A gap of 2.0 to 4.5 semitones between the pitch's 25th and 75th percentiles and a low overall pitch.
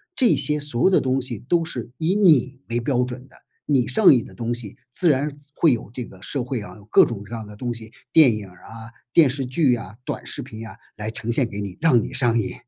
Yes: average, 4.0 semitones; low, 125 Hz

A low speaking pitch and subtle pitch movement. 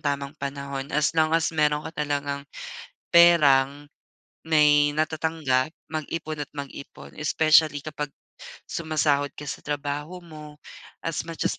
No: medium, 150 Hz; narrow, 1.8 semitones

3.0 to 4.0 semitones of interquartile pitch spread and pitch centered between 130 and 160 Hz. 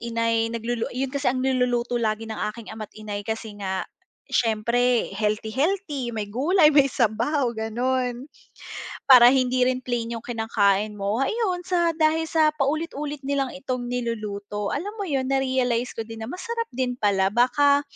No: average, 3.7 semitones; high, 245 Hz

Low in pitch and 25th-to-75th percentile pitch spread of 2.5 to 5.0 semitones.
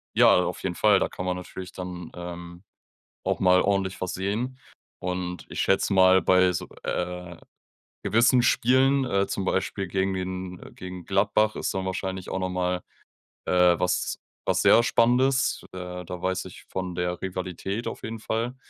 No: very low, 95 Hz; narrow, 1.8 semitones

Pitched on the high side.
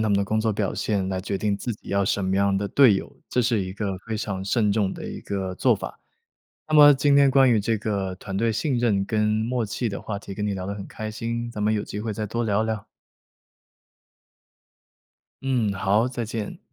No: low, 105 Hz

